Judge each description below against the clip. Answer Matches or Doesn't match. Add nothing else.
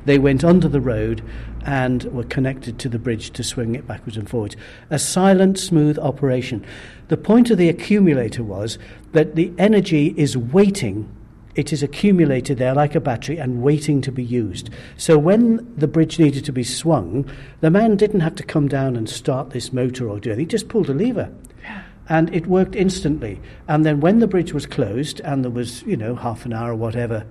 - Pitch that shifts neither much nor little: Matches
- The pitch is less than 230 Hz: Matches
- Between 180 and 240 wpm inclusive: Matches